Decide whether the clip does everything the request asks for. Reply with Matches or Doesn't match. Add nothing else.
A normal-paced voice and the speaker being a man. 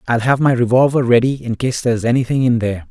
Doesn't match